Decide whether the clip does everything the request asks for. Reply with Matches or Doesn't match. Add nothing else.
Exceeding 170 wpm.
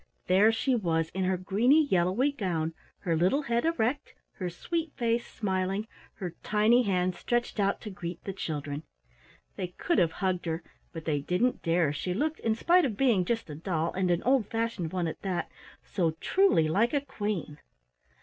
Matches